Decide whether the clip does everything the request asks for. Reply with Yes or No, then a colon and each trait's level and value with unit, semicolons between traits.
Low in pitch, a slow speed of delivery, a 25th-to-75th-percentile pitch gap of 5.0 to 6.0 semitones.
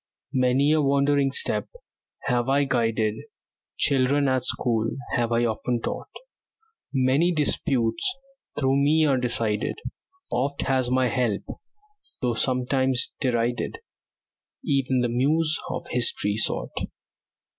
No: low, 130 Hz; slow, 115 wpm; average, 2.7 semitones